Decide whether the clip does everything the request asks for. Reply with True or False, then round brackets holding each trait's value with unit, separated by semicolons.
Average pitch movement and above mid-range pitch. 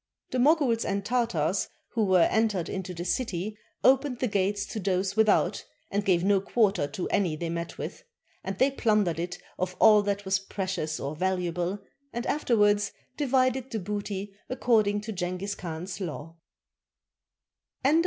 True (3.4 semitones; 200 Hz)